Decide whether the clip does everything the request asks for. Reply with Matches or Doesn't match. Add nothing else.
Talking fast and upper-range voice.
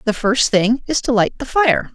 Matches